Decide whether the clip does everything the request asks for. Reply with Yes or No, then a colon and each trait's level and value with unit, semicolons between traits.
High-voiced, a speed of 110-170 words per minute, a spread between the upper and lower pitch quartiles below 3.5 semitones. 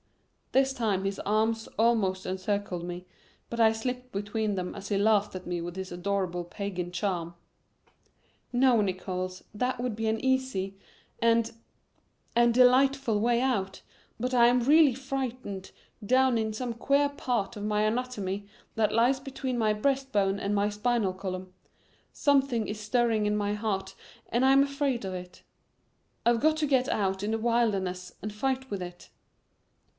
No: high, 220 Hz; average, 160 wpm; average, 4.3 semitones